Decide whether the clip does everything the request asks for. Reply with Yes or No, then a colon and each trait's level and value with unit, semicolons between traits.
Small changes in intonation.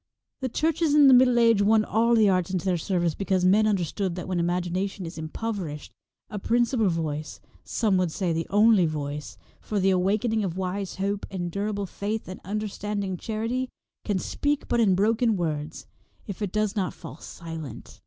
No: average, 3.7 semitones